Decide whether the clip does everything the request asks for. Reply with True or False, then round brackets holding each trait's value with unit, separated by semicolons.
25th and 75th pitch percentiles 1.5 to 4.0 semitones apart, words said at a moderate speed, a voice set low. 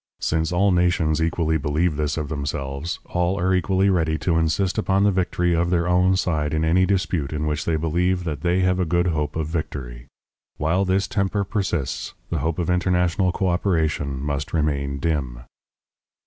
True (3.2 semitones; 175 wpm; 85 Hz)